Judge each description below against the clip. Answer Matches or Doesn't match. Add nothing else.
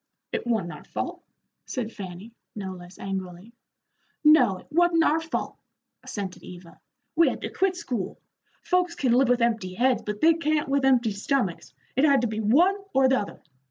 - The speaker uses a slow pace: Doesn't match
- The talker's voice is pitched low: Doesn't match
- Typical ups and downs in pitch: Doesn't match